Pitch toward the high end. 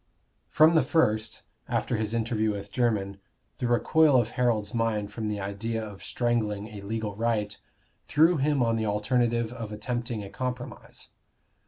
No: low, 115 Hz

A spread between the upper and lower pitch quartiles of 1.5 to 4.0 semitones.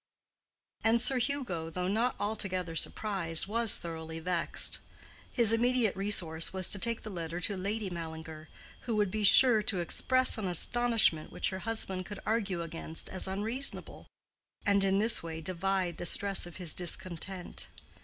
No: average, 4.4 semitones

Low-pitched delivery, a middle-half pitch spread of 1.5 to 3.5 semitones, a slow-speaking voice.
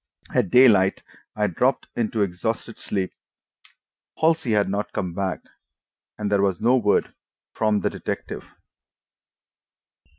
Yes: low, 105 Hz; average, 3.1 semitones; slow, 120 wpm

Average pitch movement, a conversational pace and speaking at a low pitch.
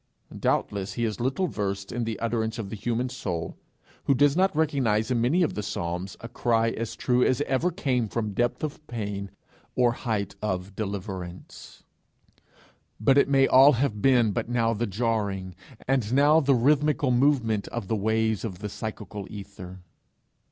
Yes: average, 4.4 semitones; average, 170 wpm; low, 115 Hz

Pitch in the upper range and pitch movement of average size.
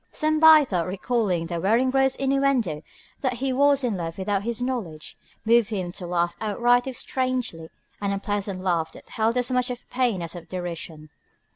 No: high, 220 Hz; wide, 6.3 semitones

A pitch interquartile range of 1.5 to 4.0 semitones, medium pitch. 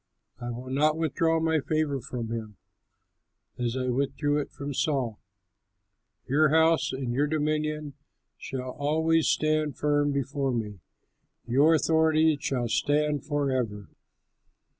Yes: average, 3.3 semitones; medium, 145 Hz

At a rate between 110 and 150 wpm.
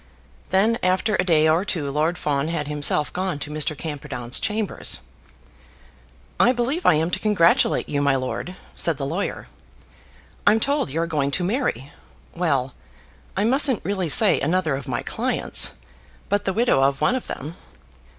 No: average, 165 wpm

